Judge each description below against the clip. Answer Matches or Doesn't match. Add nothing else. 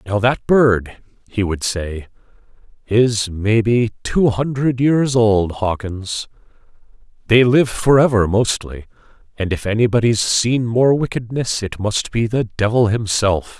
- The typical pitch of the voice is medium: Doesn't match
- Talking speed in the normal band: Doesn't match